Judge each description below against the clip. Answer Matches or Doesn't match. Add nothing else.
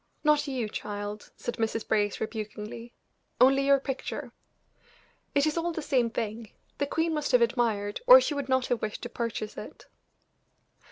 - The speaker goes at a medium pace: Matches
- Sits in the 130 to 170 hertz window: Doesn't match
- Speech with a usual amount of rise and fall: Matches